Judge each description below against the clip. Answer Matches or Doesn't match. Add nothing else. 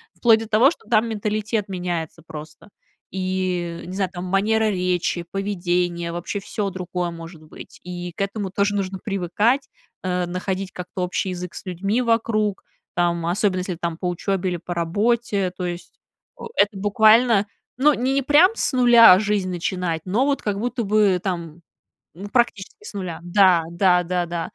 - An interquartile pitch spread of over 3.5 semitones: Doesn't match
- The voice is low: Doesn't match